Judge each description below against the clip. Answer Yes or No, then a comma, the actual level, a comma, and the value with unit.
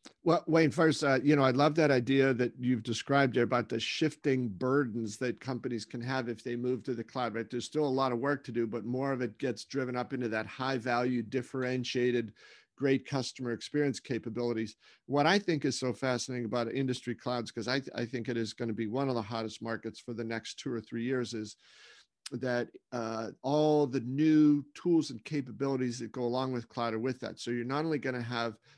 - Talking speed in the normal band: No, fast, 225 wpm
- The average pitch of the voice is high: No, low, 125 Hz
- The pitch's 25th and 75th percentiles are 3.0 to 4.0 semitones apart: No, narrow, 2.4 semitones